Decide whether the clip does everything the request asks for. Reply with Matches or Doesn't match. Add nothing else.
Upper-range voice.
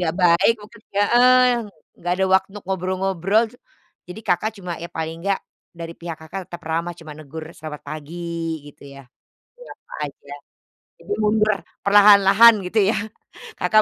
Doesn't match